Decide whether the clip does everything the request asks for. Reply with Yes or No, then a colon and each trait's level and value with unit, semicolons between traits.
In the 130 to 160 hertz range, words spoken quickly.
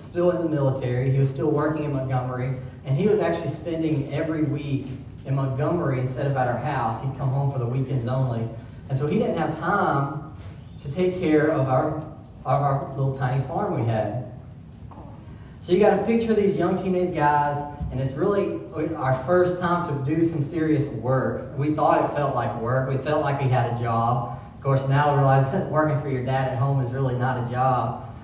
Yes: low, 135 Hz; fast, 210 wpm